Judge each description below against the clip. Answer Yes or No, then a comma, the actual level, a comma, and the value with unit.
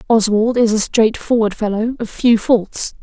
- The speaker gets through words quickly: No, average, 160 wpm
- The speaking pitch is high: Yes, high, 220 Hz